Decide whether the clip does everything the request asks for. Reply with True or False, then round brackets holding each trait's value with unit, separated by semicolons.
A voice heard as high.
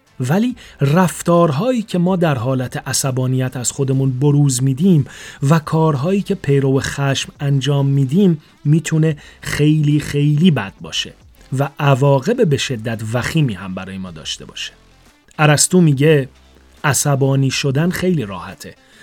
False (140 Hz)